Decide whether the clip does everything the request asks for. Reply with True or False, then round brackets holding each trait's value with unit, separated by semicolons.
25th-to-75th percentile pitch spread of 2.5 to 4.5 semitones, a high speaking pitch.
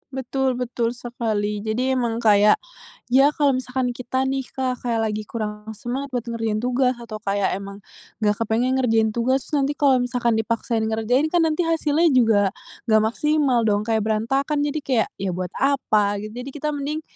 True (3.6 semitones; 245 Hz)